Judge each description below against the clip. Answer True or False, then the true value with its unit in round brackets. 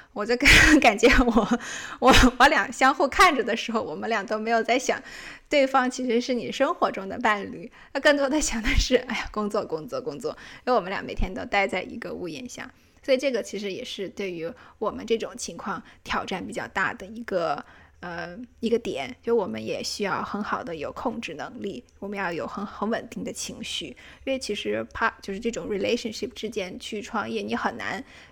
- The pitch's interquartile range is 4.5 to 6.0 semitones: False (3.6 semitones)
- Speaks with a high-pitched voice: True (230 Hz)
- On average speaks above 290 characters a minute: True (315 characters per minute)